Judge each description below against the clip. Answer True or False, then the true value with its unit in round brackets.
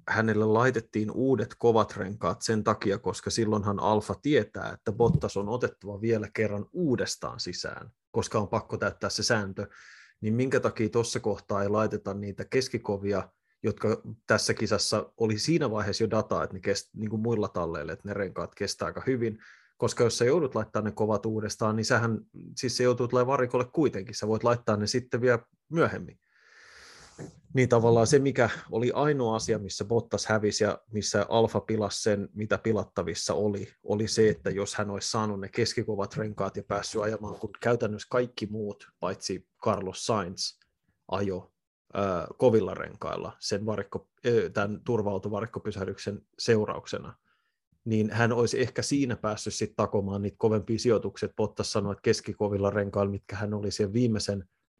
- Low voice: True (110 Hz)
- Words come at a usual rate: False (160 wpm)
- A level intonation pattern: True (2.3 semitones)